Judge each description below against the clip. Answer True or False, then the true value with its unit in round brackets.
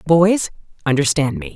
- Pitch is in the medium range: True (145 Hz)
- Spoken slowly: True (115 wpm)